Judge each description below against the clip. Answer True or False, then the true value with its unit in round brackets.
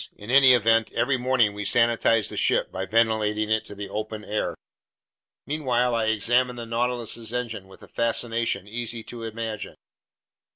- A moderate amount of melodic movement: False (2.0 semitones)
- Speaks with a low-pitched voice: True (115 Hz)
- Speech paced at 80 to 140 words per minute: False (160 wpm)